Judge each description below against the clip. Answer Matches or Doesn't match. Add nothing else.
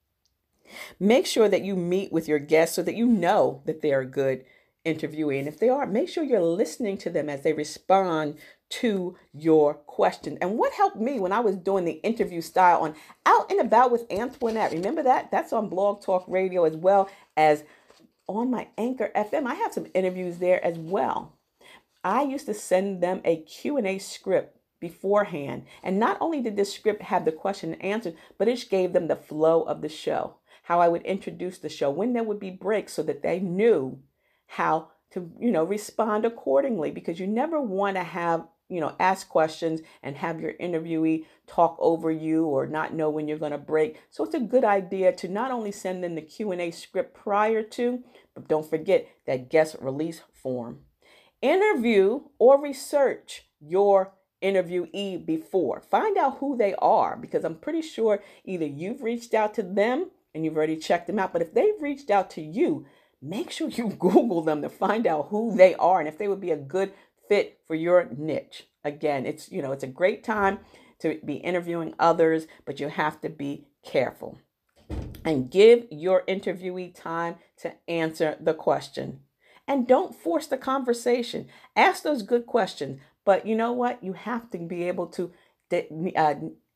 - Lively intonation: Matches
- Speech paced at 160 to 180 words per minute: Doesn't match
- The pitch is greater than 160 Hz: Matches